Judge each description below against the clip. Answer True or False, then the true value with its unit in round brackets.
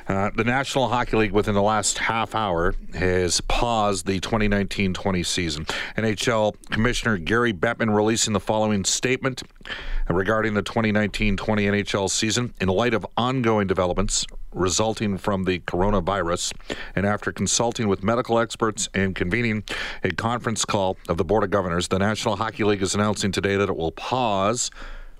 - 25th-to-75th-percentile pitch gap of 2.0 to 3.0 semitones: True (2.7 semitones)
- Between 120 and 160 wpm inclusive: True (155 wpm)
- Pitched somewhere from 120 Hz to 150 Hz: False (105 Hz)